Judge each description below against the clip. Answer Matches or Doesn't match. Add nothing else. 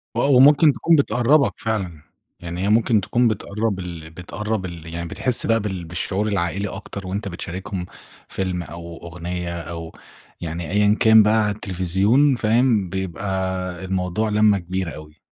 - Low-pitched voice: Matches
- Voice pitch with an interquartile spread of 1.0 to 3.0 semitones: Doesn't match